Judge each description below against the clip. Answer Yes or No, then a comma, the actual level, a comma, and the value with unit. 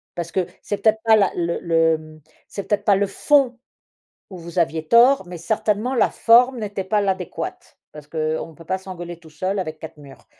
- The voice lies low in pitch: No, medium, 185 Hz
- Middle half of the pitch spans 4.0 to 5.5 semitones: Yes, average, 4.5 semitones